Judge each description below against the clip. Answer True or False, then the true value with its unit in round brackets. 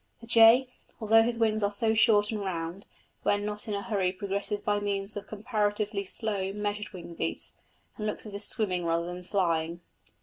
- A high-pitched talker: True (205 Hz)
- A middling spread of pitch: False (2.2 semitones)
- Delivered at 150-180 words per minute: False (190 wpm)